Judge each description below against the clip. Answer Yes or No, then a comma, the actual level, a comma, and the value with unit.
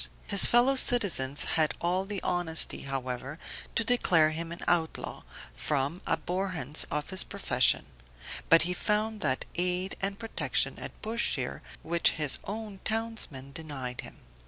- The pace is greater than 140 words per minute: No, slow, 135 wpm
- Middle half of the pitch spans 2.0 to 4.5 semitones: No, wide, 5.4 semitones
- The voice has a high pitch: No, medium, 175 Hz